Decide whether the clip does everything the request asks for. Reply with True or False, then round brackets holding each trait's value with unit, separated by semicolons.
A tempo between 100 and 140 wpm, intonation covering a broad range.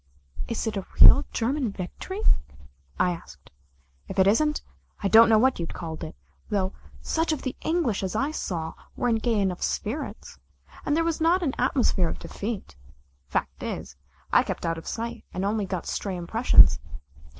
False (175 wpm; 6.4 semitones)